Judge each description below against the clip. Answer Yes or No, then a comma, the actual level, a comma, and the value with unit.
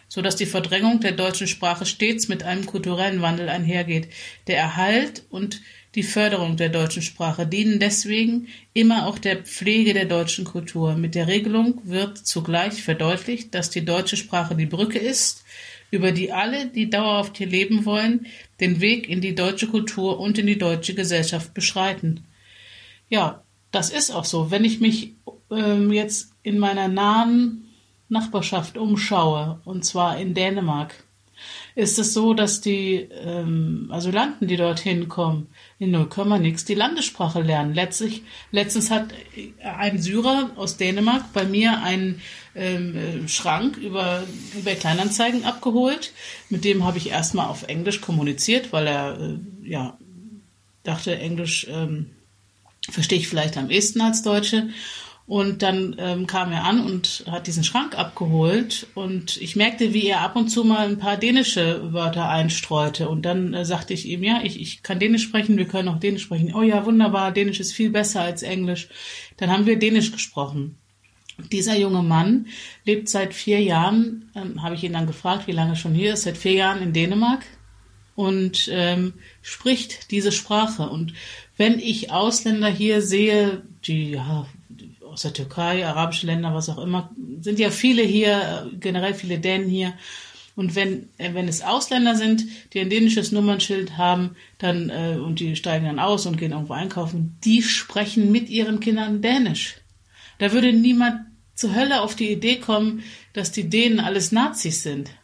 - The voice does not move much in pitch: No, average, 4.0 semitones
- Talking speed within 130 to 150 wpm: No, average, 165 wpm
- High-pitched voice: Yes, high, 195 Hz